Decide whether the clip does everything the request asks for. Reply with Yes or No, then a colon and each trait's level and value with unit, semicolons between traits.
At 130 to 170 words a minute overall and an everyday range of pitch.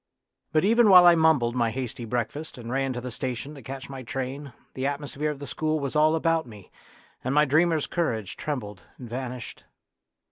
No: average, 190 wpm; average, 3.9 semitones